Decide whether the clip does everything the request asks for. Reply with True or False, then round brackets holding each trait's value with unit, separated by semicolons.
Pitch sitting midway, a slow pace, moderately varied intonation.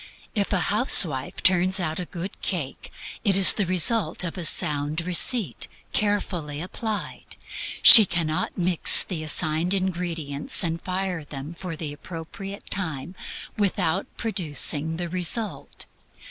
True (175 Hz; 130 wpm; 3.5 semitones)